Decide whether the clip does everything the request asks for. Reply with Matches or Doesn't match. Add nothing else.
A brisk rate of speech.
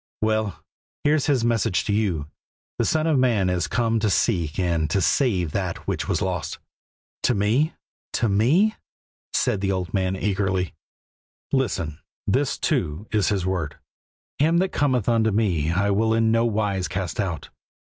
Doesn't match